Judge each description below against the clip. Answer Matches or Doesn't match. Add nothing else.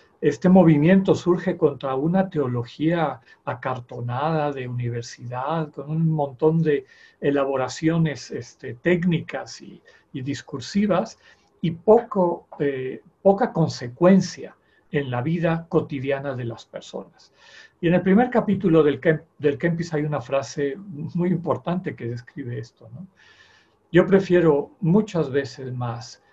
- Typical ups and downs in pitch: Matches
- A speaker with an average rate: Doesn't match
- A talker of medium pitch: Matches